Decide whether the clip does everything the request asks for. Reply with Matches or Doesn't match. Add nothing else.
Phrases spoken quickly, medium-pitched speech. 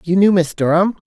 Matches